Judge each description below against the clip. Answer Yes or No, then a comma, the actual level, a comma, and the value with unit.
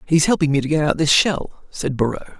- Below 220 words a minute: No, fast, 250 wpm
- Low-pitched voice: No, medium, 150 Hz